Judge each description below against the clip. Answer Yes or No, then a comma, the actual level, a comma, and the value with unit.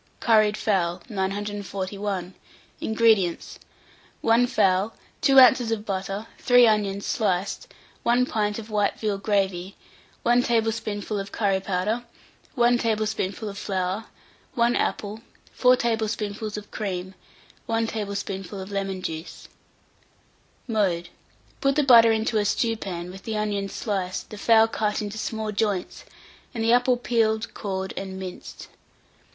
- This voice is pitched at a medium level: No, high, 210 Hz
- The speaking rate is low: Yes, slow, 130 wpm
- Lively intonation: No, narrow, 2.6 semitones